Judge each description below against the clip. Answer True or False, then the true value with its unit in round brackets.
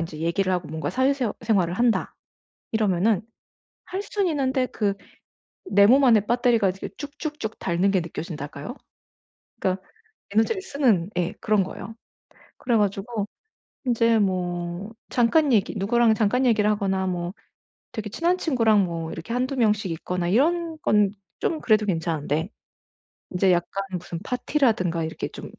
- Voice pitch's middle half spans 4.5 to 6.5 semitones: True (5.4 semitones)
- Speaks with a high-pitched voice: True (210 Hz)